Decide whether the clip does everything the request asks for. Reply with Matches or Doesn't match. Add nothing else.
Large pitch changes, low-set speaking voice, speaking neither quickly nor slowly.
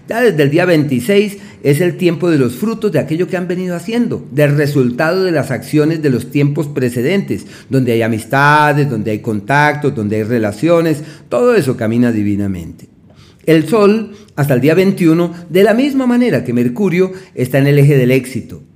Doesn't match